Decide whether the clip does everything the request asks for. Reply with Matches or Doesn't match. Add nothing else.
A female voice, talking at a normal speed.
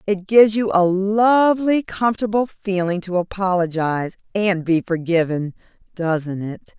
Doesn't match